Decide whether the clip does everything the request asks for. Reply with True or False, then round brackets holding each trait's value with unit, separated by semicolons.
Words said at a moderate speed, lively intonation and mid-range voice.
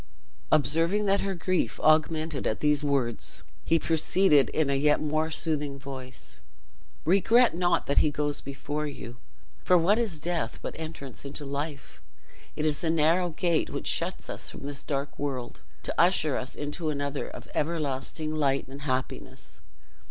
False (160 wpm; 2.8 semitones; 150 Hz)